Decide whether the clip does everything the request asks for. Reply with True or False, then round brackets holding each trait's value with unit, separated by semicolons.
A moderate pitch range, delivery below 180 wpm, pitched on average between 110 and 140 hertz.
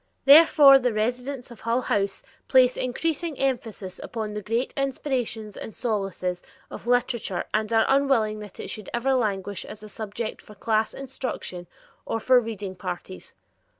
False (3.6 semitones; 150 wpm; 225 Hz)